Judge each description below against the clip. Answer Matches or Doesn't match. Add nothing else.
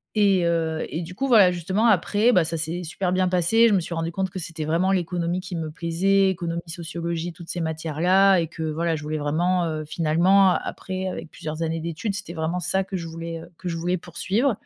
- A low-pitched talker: Doesn't match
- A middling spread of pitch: Doesn't match